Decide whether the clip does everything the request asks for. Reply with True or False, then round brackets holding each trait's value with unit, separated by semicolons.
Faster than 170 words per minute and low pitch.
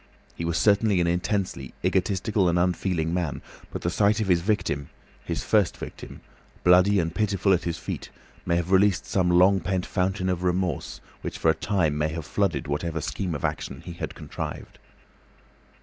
True (180 wpm; 90 Hz)